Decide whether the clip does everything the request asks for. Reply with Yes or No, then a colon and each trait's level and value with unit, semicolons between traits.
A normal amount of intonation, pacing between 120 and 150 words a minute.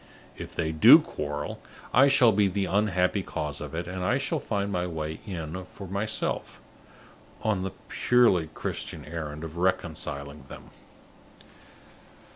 Yes: average, 4.4 semitones; average, 140 wpm